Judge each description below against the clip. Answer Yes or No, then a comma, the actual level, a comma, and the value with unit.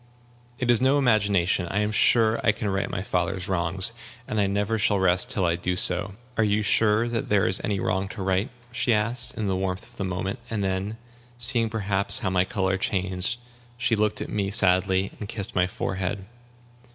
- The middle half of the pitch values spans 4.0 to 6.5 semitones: No, narrow, 2.6 semitones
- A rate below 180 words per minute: No, fast, 205 wpm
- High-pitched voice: No, low, 100 Hz